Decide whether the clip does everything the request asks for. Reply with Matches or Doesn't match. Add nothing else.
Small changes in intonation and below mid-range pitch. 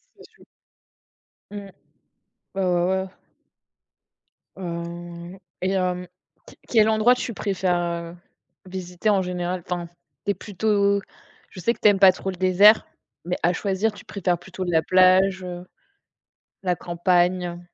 Doesn't match